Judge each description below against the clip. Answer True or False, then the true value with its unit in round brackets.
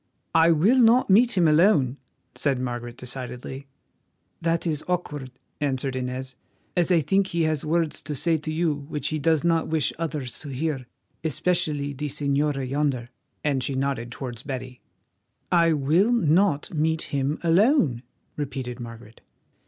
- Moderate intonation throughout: True (4.0 semitones)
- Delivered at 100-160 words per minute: True (150 wpm)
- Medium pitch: True (150 Hz)